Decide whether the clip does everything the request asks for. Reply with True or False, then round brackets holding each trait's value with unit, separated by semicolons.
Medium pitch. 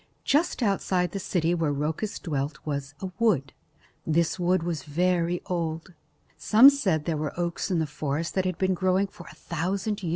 True (175 Hz)